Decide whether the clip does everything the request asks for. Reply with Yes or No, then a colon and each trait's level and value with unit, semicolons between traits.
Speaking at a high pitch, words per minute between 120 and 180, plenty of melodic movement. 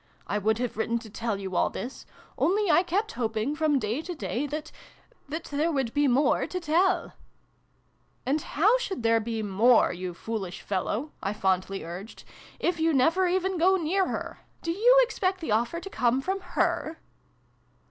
No: very high, 285 Hz; average, 190 wpm; wide, 8.0 semitones